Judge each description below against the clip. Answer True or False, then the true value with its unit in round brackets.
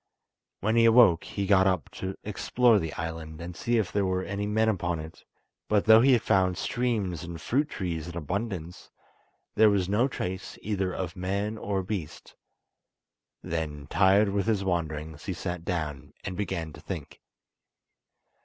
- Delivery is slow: False (165 wpm)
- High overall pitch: False (95 Hz)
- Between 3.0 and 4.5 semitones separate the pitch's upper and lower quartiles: True (3.7 semitones)